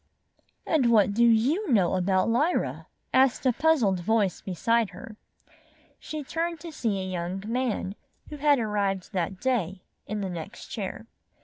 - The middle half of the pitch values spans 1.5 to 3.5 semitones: No, wide, 5.4 semitones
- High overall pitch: Yes, high, 220 Hz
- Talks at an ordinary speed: Yes, average, 150 wpm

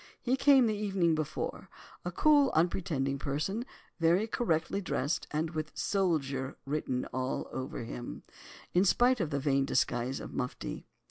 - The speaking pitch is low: No, medium, 160 Hz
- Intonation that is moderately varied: No, wide, 6.6 semitones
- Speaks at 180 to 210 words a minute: No, slow, 135 wpm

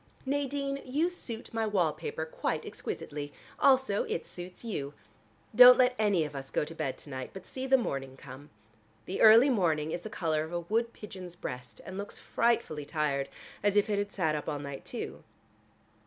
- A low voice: No, medium, 185 Hz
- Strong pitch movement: Yes, wide, 7.5 semitones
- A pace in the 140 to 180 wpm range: No, average, 190 wpm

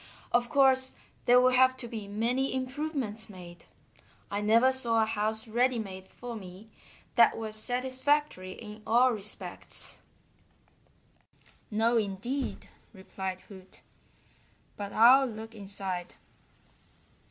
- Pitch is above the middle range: Yes, high, 225 Hz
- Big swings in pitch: No, average, 3.9 semitones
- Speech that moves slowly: Yes, slow, 115 wpm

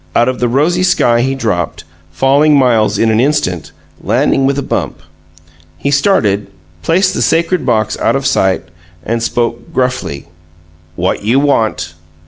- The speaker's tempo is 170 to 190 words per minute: No, average, 150 wpm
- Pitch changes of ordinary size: Yes, average, 4.5 semitones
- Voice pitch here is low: Yes, low, 125 Hz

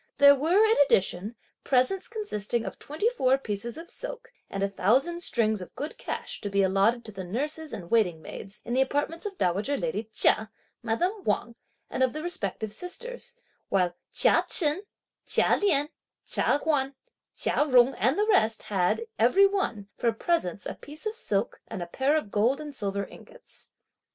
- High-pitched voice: Yes, very high, 260 Hz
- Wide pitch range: Yes, wide, 8.5 semitones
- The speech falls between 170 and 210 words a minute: Yes, average, 175 wpm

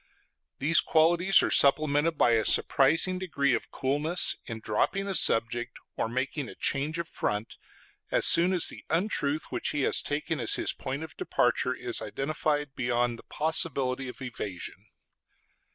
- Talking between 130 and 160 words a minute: Yes, average, 155 wpm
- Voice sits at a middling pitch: Yes, medium, 145 Hz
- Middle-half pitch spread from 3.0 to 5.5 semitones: Yes, average, 4.4 semitones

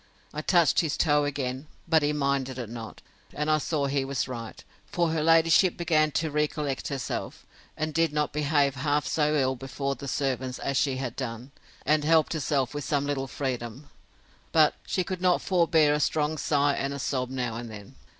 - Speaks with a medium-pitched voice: Yes, medium, 145 Hz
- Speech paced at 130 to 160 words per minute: No, average, 190 wpm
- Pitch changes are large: No, average, 2.7 semitones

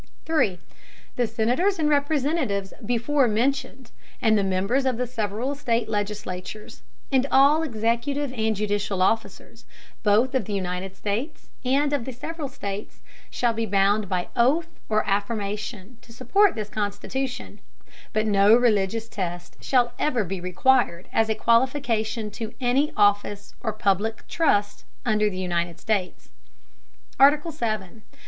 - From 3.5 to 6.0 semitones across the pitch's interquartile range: Yes, average, 4.4 semitones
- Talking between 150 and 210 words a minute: No, slow, 135 wpm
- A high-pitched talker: Yes, high, 225 Hz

